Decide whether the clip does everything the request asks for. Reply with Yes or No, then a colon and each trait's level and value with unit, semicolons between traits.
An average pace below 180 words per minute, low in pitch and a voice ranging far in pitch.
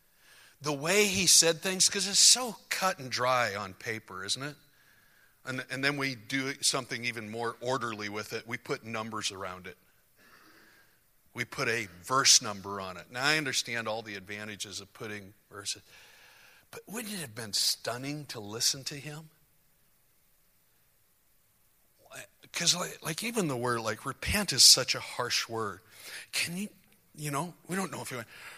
Yes: average, 170 wpm; low, 130 Hz; wide, 6.0 semitones